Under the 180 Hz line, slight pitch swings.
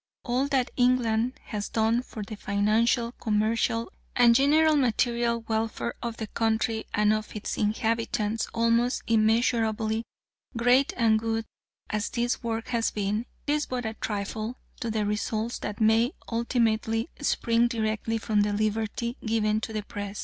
No: high, 225 Hz; narrow, 1.6 semitones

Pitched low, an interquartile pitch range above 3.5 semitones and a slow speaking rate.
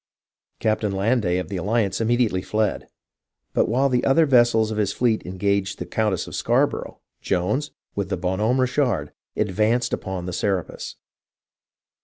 No: low, 105 Hz; average, 4.1 semitones; average, 155 wpm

